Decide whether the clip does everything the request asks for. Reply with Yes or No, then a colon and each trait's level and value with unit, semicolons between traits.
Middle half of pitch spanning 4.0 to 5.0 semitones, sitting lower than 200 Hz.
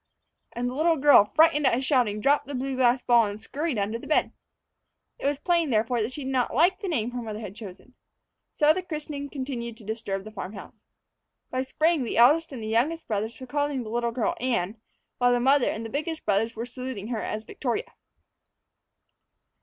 No: average, 4.5 semitones; very high, 250 Hz